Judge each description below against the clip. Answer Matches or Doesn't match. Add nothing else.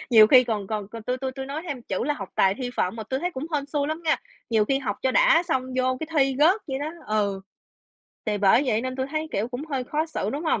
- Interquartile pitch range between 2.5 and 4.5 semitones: Doesn't match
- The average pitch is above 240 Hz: Matches